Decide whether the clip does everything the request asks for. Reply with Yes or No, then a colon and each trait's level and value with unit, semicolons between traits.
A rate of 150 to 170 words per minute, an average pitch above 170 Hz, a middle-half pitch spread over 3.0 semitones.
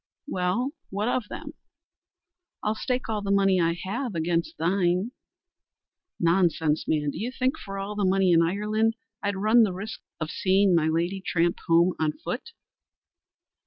Yes: average, 160 wpm; high, 190 Hz; average, 3.9 semitones